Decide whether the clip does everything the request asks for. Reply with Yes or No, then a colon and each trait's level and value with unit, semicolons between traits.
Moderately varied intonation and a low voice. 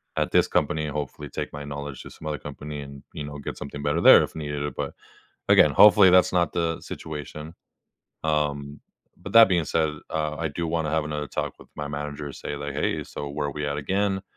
No: narrow, 1.8 semitones; very low, 75 Hz